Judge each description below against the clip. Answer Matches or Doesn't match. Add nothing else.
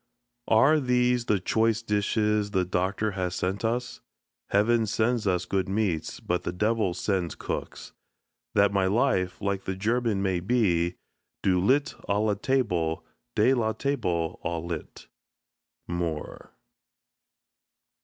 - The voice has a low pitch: Matches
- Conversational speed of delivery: Doesn't match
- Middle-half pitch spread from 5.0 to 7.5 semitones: Doesn't match